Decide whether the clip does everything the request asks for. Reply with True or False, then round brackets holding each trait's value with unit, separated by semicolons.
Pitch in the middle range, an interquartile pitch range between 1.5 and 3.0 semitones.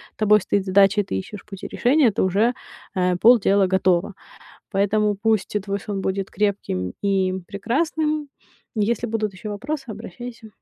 False (205 Hz; 2.7 semitones)